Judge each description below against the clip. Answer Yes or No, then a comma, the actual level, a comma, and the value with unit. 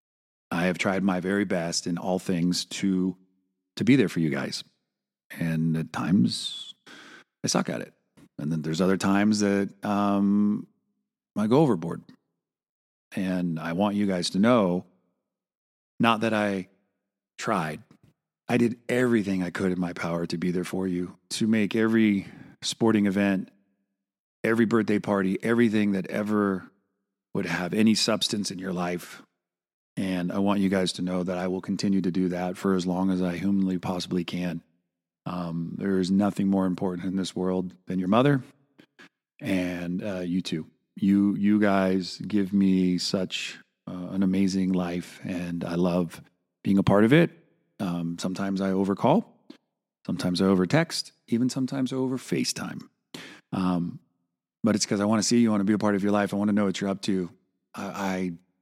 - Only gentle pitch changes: Yes, narrow, 2.1 semitones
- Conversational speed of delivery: Yes, average, 175 wpm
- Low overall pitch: Yes, very low, 95 Hz